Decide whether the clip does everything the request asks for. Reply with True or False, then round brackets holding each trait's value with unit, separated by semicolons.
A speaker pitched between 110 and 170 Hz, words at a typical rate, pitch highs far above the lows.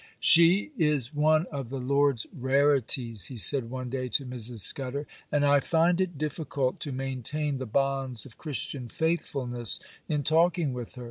False (135 Hz; 160 wpm; 3.0 semitones)